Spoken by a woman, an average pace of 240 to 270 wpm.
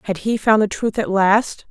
Yes: female; fast, 245 wpm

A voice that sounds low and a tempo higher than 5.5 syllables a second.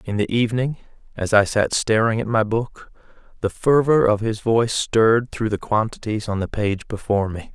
No: low, 110 Hz; 5.2 syllables/s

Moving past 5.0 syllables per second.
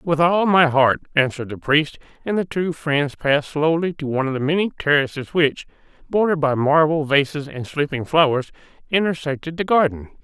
Yes: 5.4 syllables/s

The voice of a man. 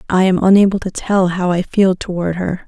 No: female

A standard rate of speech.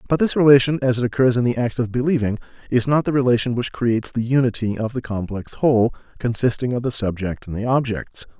No: fast, 215 wpm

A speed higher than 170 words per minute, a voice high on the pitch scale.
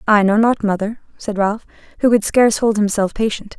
Yes: average, 200 wpm; high, 215 Hz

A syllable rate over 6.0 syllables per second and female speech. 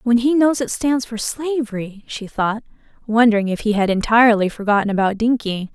No: 5.4 syllables/s; female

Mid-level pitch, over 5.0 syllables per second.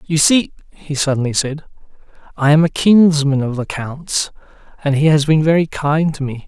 No: medium, 150 Hz; 4.9 syllables/s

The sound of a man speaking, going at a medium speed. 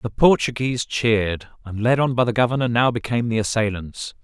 Yes: male; average, 185 wpm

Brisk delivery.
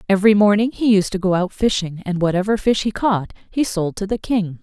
Yes: fast, 235 wpm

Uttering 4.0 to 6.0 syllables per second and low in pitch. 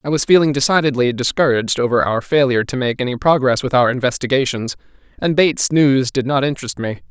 No: 6.3 syllables/s; low, 130 Hz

